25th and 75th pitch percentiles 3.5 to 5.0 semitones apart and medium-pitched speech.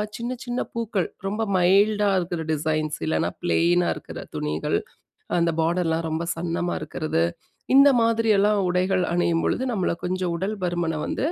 Yes: average, 3.9 semitones; medium, 175 Hz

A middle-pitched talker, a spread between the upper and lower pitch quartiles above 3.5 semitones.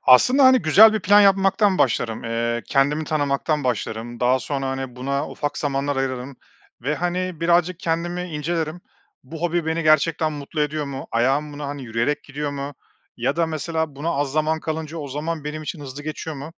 No: medium, 150 Hz; average, 3.2 semitones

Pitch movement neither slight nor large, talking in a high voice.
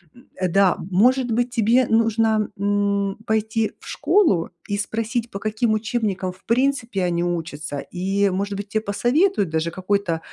Yes: average, 3.2 semitones; high, 205 Hz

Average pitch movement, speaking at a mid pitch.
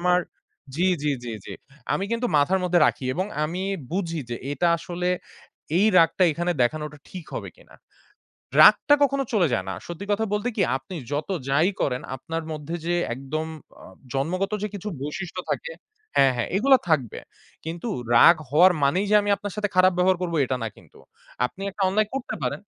Yes: average, 4.7 semitones; medium, 175 Hz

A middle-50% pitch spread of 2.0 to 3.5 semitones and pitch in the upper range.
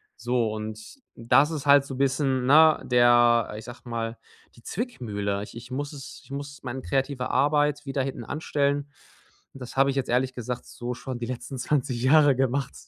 No: average, 2.7 semitones; low, 130 Hz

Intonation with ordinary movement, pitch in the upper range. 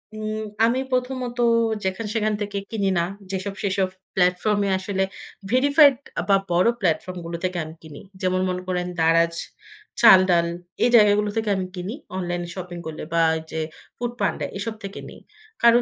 Yes: average, 3.6 semitones; high, 195 Hz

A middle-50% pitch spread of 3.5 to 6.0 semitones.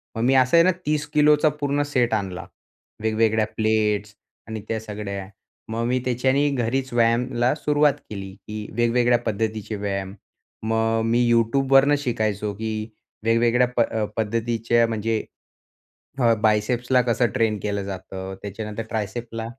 No: narrow, 2.6 semitones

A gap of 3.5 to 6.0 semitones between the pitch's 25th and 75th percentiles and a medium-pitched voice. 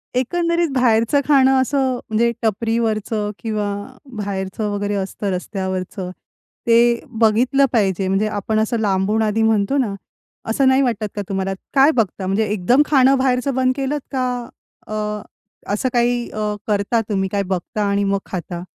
No: average, 4.1 semitones; high, 220 Hz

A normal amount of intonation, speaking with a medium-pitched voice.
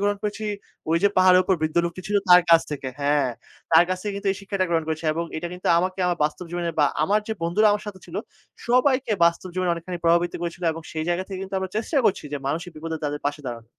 Yes: average, 3.2 semitones; medium, 175 Hz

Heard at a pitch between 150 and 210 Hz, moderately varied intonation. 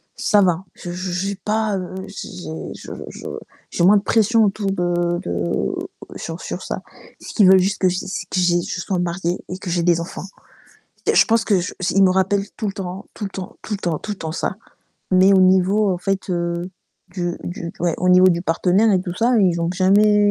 No: medium, 185 Hz; narrow, 2.2 semitones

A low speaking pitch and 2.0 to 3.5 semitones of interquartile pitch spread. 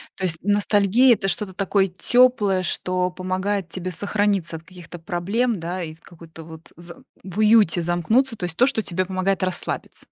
No: medium, 185 Hz; average, 2.9 semitones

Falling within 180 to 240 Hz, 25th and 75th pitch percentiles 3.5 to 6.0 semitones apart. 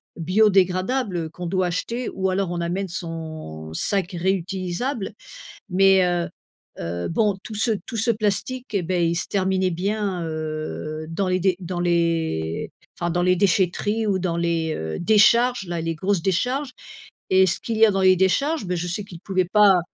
No: medium, 185 Hz; average, 3.0 semitones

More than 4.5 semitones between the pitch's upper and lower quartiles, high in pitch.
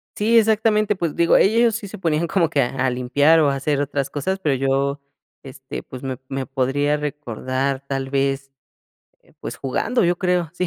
No: average, 5.0 semitones; medium, 145 Hz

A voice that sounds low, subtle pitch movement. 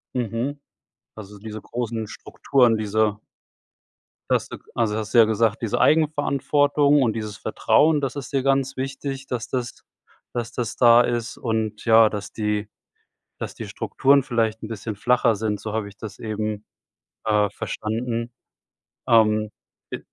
No: low, 115 Hz; average, 3.1 semitones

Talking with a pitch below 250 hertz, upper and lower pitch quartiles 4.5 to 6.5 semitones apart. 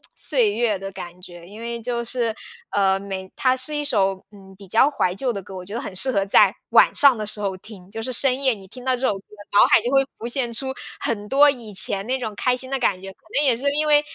Yes: high, 225 Hz; average, 4.9 semitones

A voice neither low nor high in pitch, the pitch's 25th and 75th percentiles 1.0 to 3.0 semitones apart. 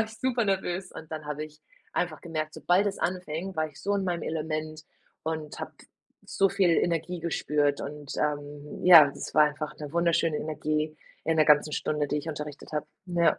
Yes: medium, 155 Hz; narrow, 2.6 semitones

